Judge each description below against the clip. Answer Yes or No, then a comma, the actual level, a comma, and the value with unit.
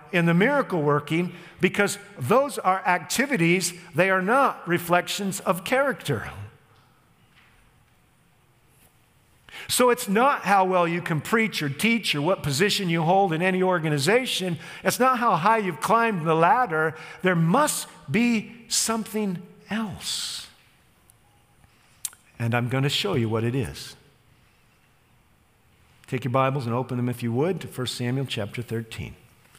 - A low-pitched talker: No, medium, 175 Hz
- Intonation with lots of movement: Yes, wide, 7.2 semitones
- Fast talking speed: No, average, 140 wpm